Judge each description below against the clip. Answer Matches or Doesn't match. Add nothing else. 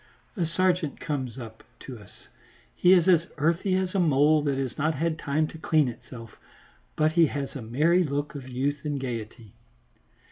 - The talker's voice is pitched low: Doesn't match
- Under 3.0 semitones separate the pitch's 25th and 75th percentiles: Doesn't match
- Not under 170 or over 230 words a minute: Matches